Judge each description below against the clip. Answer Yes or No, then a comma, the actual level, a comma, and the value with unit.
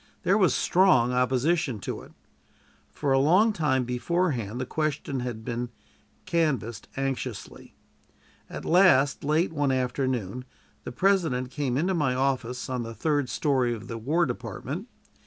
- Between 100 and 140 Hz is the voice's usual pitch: Yes, low, 135 Hz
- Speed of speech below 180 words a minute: Yes, average, 140 wpm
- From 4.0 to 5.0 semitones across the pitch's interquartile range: Yes, average, 4.4 semitones